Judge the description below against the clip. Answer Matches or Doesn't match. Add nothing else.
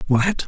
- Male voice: Matches